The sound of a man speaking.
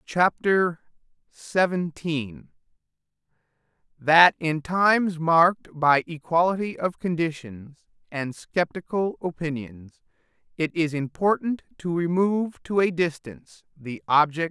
Yes: male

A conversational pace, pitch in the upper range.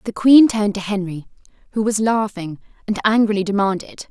Yes: average, 160 wpm; high, 205 Hz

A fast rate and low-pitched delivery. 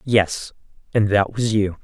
No: average, 165 wpm; low, 105 Hz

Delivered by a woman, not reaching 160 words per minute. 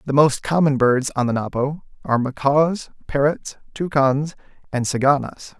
No: male; average, 140 wpm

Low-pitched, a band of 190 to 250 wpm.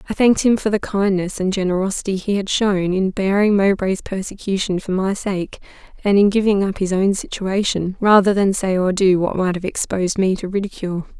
No: high, 195 Hz; average, 200 wpm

